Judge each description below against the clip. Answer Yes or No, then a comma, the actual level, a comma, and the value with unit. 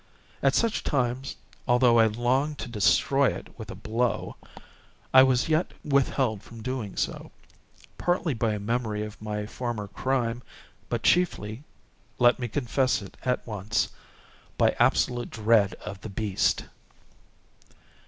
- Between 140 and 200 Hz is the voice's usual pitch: No, low, 120 Hz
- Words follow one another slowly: Yes, slow, 130 wpm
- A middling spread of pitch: Yes, average, 3.6 semitones